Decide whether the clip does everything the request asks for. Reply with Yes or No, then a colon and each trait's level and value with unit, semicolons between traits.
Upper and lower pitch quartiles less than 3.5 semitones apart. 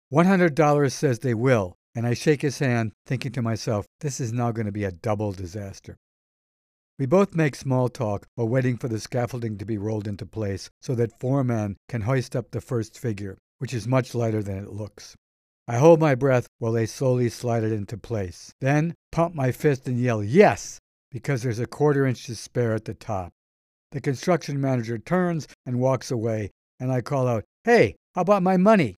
No: average, 3.8 semitones